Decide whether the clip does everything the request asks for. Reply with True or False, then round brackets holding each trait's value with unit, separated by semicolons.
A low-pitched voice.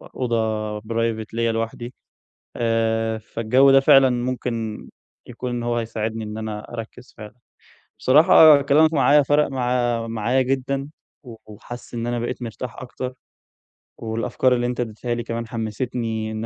True (120 Hz)